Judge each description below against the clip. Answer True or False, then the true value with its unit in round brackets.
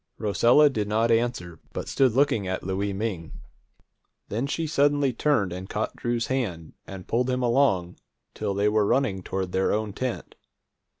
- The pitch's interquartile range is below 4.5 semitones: False (4.9 semitones)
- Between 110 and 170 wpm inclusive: True (165 wpm)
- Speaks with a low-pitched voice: True (110 Hz)